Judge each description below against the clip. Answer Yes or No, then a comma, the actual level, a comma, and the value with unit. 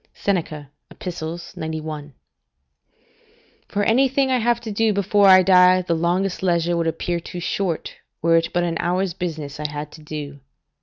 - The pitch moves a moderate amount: Yes, average, 3.5 semitones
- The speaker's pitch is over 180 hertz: No, medium, 175 Hz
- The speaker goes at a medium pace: Yes, average, 160 wpm